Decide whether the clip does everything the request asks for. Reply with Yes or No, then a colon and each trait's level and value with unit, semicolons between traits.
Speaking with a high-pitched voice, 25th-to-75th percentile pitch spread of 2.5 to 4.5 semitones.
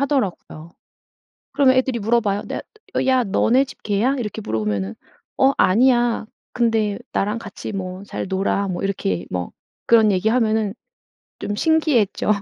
Yes: high, 215 Hz; average, 4.0 semitones